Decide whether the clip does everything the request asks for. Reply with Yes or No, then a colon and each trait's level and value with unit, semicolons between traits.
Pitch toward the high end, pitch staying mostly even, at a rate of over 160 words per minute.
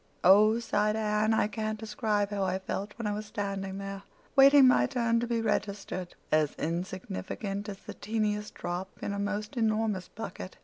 Yes: high, 210 Hz; narrow, 2.1 semitones; average, 170 wpm